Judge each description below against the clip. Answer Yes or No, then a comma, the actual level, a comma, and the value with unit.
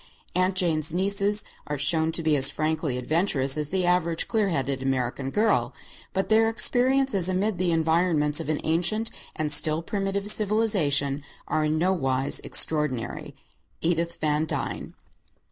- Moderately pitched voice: Yes, medium, 165 Hz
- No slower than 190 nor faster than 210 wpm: No, average, 145 wpm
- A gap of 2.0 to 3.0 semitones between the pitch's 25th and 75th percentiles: No, average, 4.6 semitones